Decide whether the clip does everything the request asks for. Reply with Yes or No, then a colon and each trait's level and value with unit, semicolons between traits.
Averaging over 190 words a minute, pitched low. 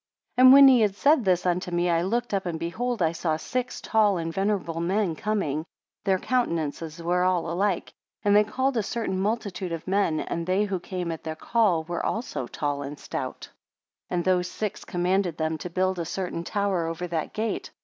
No: fast, 205 wpm; medium, 185 Hz